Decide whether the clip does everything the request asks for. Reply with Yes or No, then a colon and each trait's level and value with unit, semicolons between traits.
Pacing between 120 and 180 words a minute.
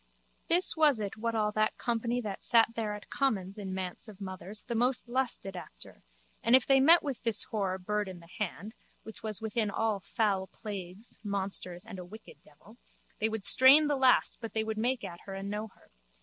No: fast, 205 wpm